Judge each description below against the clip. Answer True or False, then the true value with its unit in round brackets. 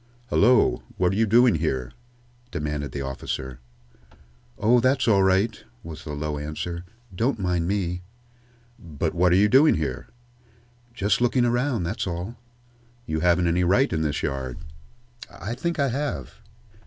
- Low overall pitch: True (90 Hz)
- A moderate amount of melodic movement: False (7.0 semitones)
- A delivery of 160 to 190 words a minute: False (150 wpm)